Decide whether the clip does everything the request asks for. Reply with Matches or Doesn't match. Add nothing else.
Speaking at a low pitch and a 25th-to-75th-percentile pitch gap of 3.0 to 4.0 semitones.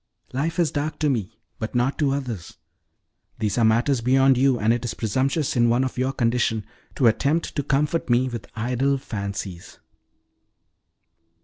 Matches